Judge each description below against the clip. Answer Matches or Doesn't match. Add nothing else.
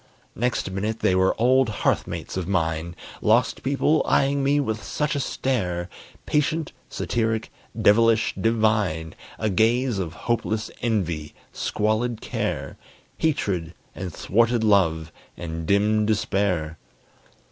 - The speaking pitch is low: Matches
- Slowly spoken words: Matches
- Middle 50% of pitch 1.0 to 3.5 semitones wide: Doesn't match